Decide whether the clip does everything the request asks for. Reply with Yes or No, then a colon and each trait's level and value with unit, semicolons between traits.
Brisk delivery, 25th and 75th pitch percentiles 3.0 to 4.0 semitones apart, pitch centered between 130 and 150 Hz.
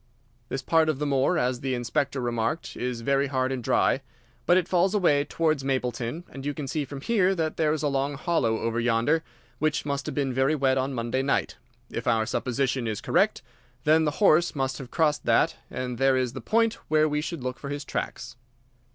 Yes: fast, 210 wpm; average, 3.3 semitones; medium, 140 Hz